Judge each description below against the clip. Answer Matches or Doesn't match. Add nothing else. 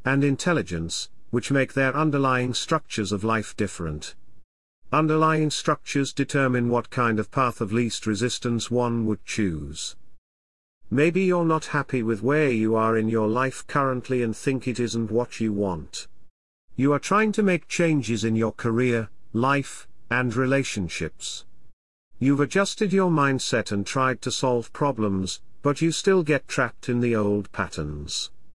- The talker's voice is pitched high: Doesn't match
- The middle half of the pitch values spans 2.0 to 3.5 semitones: Doesn't match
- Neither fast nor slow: Matches